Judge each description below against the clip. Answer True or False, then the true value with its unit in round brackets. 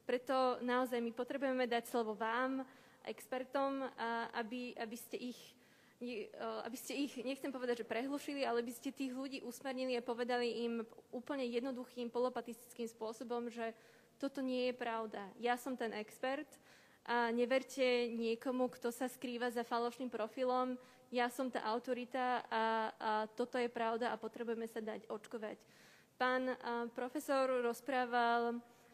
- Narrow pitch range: True (1.6 semitones)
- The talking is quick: False (140 wpm)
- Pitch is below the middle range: False (245 Hz)